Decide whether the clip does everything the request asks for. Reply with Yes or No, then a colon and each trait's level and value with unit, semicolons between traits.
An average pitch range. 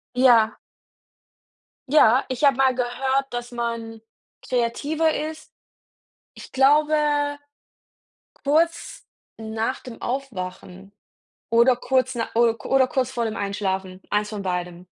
Yes: average, 3.7 semitones